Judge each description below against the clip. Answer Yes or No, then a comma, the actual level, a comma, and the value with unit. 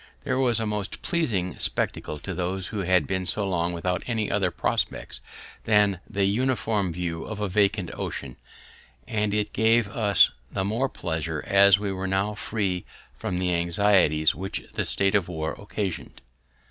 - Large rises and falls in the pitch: No, average, 2.8 semitones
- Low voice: Yes, low, 100 Hz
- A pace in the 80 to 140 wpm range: No, average, 165 wpm